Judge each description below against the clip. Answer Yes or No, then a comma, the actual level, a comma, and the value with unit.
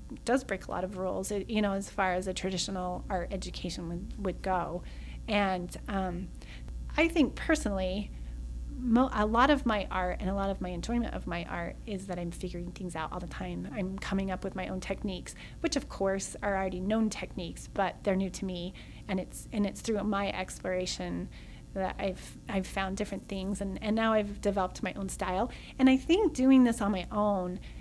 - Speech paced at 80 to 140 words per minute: No, fast, 205 wpm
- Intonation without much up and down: Yes, narrow, 2.3 semitones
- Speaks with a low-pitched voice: No, high, 195 Hz